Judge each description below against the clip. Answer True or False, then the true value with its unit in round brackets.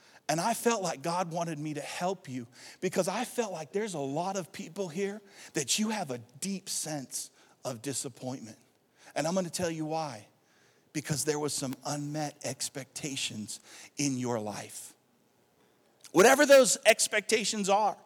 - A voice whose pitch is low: False (165 Hz)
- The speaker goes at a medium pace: True (160 wpm)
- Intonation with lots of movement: True (6.0 semitones)